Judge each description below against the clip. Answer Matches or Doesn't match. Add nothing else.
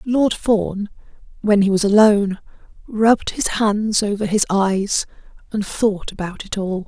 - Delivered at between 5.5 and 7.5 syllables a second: Doesn't match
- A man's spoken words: Doesn't match